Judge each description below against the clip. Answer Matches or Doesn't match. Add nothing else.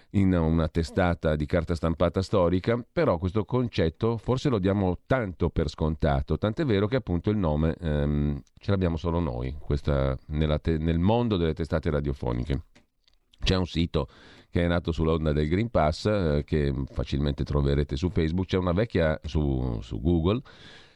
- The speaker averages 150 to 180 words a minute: Matches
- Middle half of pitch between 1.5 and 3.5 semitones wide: Doesn't match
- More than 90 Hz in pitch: Doesn't match